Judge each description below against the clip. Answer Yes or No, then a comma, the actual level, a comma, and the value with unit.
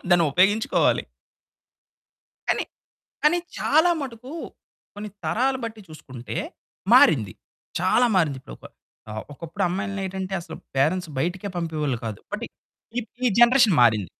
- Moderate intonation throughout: No, wide, 6.5 semitones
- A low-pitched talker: No, medium, 185 Hz